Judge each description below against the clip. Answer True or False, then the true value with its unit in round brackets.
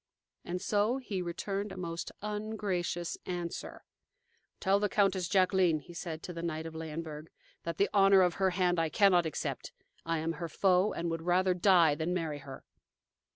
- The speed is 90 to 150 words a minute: False (175 wpm)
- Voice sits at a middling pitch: True (175 Hz)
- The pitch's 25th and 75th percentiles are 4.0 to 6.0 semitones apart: False (2.8 semitones)